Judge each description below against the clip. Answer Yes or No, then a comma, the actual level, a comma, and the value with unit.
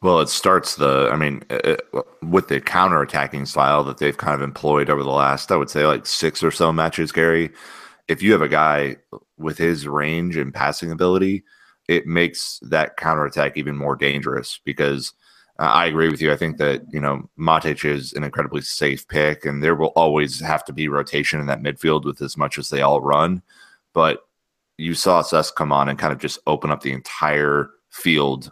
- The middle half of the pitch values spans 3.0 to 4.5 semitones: No, narrow, 2.4 semitones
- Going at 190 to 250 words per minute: Yes, average, 200 wpm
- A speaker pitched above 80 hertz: No, very low, 75 Hz